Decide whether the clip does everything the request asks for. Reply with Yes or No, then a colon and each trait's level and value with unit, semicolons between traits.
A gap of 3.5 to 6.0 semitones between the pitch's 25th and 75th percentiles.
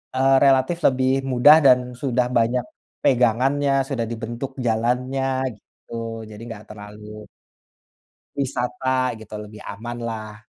No: average, 2.9 semitones